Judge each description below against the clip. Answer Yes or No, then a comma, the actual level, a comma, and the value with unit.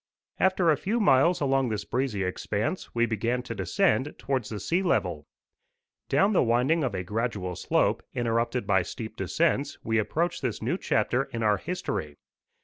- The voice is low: Yes, low, 125 Hz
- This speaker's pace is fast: No, average, 165 wpm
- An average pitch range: No, wide, 6.0 semitones